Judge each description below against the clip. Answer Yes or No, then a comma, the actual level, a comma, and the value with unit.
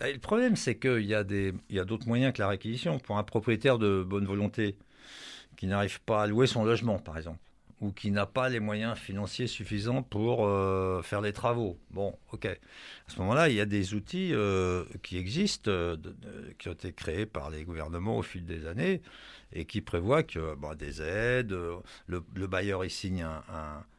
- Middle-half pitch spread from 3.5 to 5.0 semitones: Yes, average, 4.0 semitones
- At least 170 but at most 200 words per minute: No, average, 210 wpm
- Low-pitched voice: Yes, low, 100 Hz